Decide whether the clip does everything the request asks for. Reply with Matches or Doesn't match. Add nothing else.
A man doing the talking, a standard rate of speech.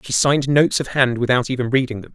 Doesn't match